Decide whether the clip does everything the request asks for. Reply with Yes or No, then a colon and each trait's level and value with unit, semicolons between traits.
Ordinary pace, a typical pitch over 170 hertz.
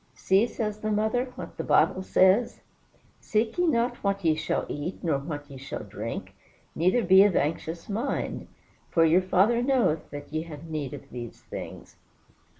Yes: average, 170 wpm; medium, 185 Hz